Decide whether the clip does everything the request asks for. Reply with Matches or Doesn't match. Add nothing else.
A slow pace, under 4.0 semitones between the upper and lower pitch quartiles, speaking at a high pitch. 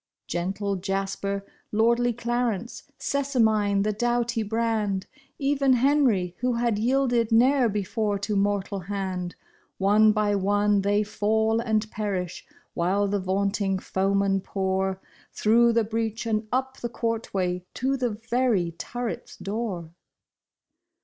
Matches